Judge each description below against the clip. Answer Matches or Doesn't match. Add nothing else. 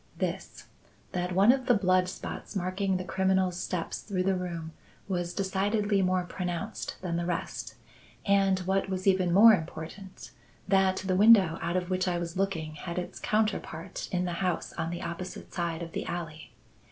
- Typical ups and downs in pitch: Doesn't match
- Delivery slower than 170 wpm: Doesn't match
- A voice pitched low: Doesn't match